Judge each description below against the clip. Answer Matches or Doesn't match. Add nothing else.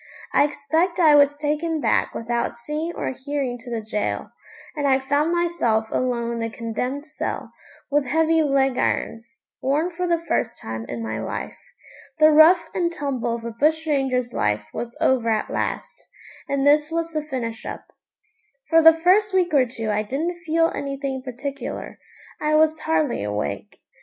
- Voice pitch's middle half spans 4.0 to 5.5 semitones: Matches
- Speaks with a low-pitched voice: Doesn't match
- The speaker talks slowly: Doesn't match